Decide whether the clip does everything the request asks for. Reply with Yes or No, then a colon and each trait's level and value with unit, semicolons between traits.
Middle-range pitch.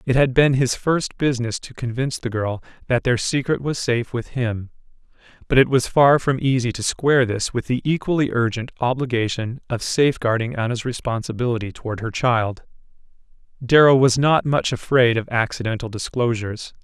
No: low, 125 Hz